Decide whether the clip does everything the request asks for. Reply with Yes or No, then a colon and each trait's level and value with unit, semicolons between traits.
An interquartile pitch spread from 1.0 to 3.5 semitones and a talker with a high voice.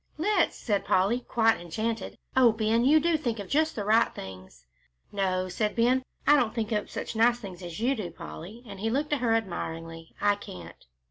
No: average, 4.6 semitones; high, 220 Hz